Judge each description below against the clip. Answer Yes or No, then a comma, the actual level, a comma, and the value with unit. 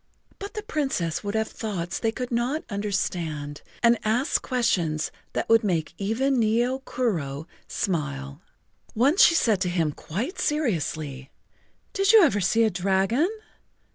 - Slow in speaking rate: No, average, 145 wpm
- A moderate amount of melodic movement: No, wide, 7.0 semitones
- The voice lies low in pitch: No, high, 215 Hz